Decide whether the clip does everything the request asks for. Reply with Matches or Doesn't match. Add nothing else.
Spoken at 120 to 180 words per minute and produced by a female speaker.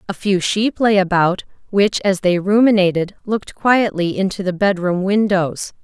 Matches